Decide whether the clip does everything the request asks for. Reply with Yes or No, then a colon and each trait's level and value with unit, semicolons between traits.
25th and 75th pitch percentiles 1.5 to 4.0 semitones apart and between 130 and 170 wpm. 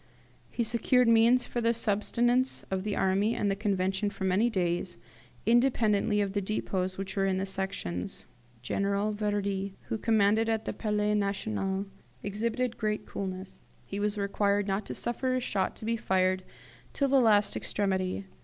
Yes: narrow, 2.6 semitones; average, 165 wpm